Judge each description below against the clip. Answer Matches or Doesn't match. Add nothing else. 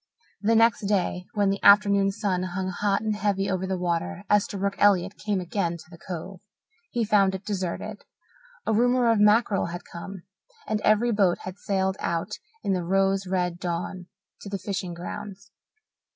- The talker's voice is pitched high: Matches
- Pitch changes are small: Matches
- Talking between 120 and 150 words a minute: Doesn't match